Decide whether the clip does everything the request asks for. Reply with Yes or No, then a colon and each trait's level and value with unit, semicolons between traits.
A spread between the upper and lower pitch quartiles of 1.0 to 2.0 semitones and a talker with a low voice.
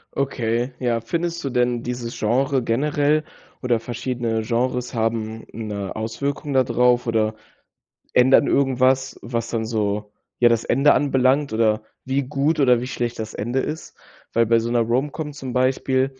No: average, 2.7 semitones; low, 125 Hz